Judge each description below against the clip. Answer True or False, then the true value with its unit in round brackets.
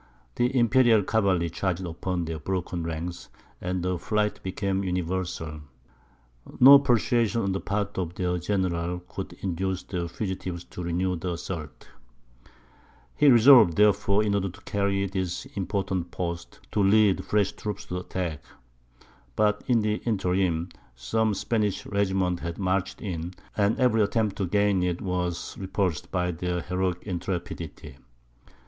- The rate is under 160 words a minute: True (140 wpm)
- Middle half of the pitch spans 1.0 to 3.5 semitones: True (2.7 semitones)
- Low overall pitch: True (95 Hz)